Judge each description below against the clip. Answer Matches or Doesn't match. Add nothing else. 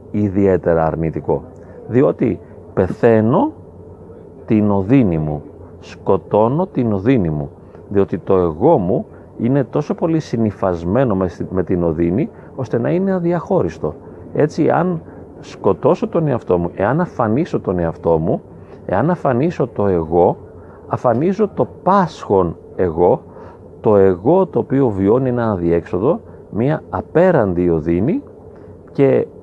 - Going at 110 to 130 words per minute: Matches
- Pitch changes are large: Matches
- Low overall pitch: Matches